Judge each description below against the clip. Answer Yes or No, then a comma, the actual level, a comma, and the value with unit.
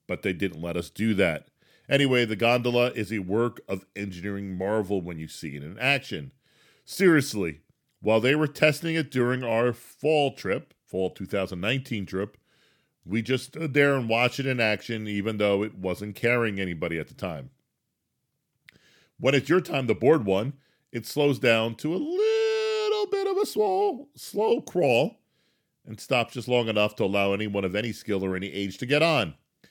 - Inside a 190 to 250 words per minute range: No, average, 180 wpm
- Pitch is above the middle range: No, low, 115 Hz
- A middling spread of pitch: No, wide, 6.3 semitones